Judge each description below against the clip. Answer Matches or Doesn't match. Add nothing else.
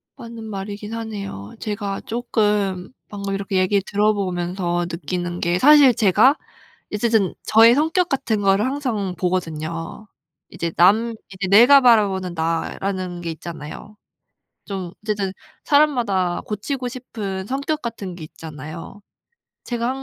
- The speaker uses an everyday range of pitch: Matches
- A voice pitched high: Matches